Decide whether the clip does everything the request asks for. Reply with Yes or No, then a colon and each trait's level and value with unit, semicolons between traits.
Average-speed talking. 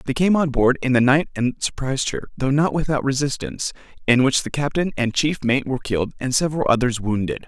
No: fast, 215 wpm